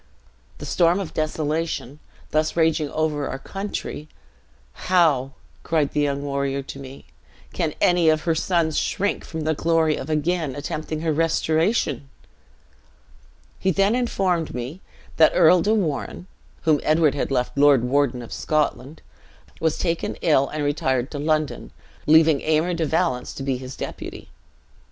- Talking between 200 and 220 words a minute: No, average, 145 wpm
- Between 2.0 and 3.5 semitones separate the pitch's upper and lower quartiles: Yes, average, 2.7 semitones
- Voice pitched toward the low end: No, medium, 155 Hz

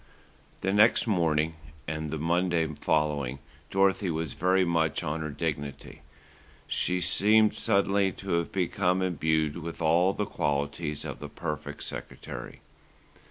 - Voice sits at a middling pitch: No, very low, 85 Hz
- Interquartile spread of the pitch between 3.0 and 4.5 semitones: Yes, average, 3.4 semitones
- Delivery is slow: Yes, slow, 130 wpm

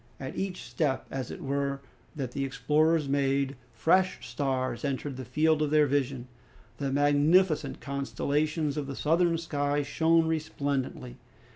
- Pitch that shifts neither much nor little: No, narrow, 2.3 semitones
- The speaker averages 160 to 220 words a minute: No, average, 140 wpm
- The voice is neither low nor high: Yes, medium, 145 Hz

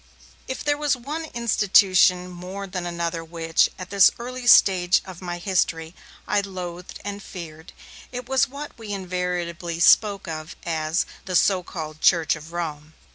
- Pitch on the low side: No, medium, 180 Hz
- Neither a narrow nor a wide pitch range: Yes, average, 3.2 semitones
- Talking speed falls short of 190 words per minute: Yes, average, 155 wpm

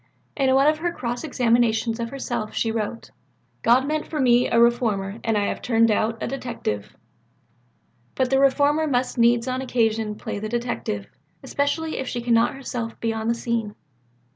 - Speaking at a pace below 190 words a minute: Yes, average, 175 wpm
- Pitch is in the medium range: No, high, 240 Hz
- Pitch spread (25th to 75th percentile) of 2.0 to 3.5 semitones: Yes, average, 2.8 semitones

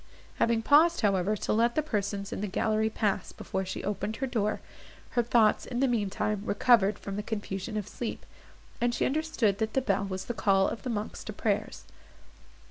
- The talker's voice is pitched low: No, high, 215 Hz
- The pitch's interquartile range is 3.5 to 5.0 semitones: No, average, 3.1 semitones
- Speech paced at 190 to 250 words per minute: Yes, average, 200 wpm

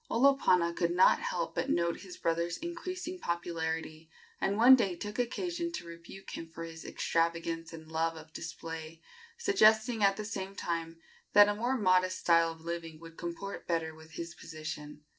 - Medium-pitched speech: Yes, medium, 170 Hz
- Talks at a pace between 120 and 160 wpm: No, average, 170 wpm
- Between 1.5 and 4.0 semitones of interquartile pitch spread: No, average, 4.4 semitones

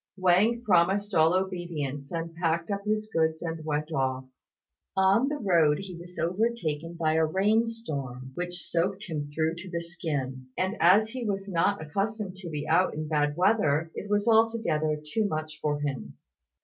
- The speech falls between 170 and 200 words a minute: Yes, average, 175 wpm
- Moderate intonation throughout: Yes, average, 4.4 semitones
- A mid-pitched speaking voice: Yes, medium, 170 Hz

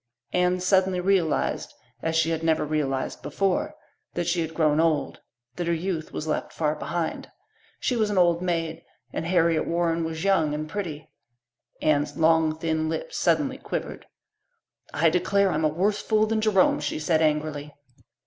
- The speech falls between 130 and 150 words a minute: No, average, 165 wpm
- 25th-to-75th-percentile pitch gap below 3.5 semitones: Yes, narrow, 2.5 semitones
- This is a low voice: No, medium, 165 Hz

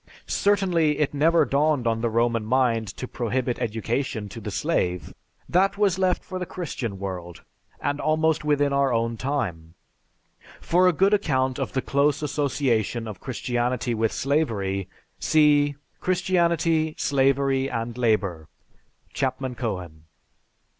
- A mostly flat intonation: No, average, 5.1 semitones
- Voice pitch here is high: No, low, 130 Hz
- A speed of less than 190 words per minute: Yes, slow, 135 wpm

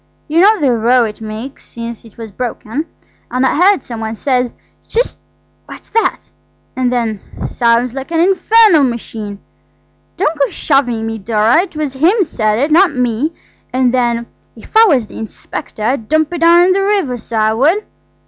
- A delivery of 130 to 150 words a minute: No, average, 175 wpm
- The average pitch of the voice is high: Yes, very high, 255 Hz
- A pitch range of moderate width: No, wide, 6.3 semitones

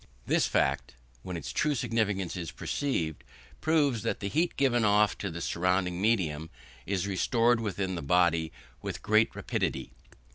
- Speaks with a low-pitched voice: Yes, low, 100 Hz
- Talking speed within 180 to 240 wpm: No, average, 150 wpm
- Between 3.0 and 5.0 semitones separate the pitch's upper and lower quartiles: Yes, average, 4.7 semitones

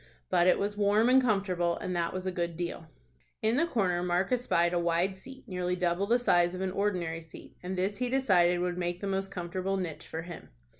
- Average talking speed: No, fast, 220 wpm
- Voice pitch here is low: No, medium, 185 Hz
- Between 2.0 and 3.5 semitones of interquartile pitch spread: Yes, narrow, 2.6 semitones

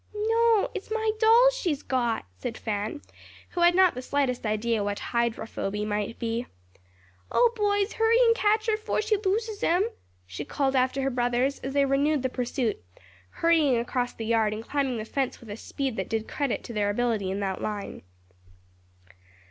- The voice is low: No, very high, 260 Hz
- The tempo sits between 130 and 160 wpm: No, average, 180 wpm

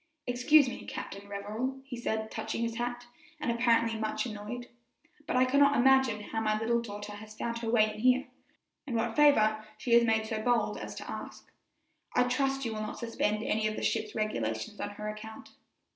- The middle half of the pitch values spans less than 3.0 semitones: Yes, narrow, 2.4 semitones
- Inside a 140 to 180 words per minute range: No, average, 195 wpm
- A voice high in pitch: Yes, high, 225 Hz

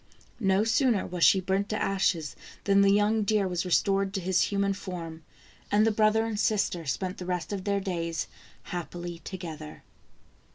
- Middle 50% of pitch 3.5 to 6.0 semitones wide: No, average, 2.7 semitones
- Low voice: No, high, 195 Hz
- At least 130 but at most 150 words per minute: No, average, 170 wpm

